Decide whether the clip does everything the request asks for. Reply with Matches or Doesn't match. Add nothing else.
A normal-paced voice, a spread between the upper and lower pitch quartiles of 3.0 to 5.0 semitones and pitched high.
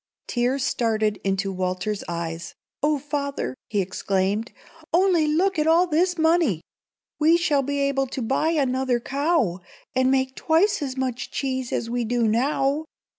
Doesn't match